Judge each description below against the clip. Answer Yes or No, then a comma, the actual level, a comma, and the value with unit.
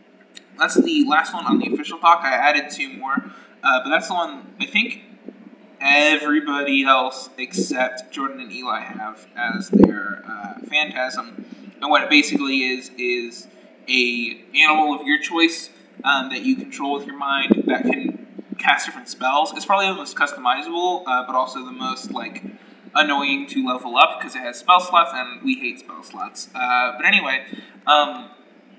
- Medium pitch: Yes, medium, 150 Hz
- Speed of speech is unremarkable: Yes, average, 170 wpm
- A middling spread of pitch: No, wide, 8.6 semitones